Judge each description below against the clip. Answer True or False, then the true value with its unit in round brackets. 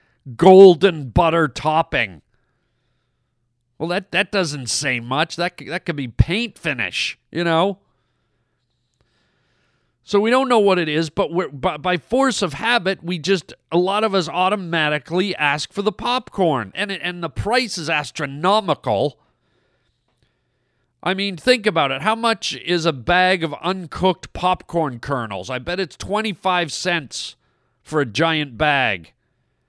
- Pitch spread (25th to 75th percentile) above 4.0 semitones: True (4.6 semitones)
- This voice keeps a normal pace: True (145 wpm)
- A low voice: False (175 Hz)